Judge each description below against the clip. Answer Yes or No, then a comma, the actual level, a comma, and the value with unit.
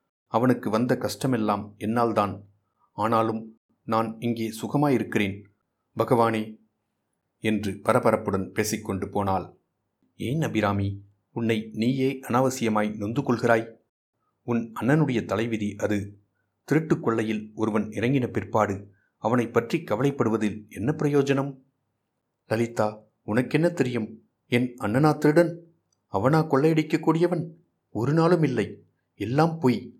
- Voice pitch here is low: Yes, low, 115 Hz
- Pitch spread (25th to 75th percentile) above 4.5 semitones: No, average, 3.8 semitones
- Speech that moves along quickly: No, average, 90 wpm